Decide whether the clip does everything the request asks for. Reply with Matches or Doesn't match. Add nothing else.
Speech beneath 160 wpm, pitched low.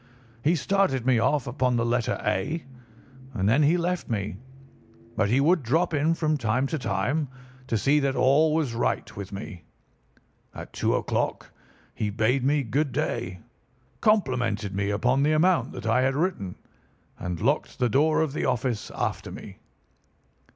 Doesn't match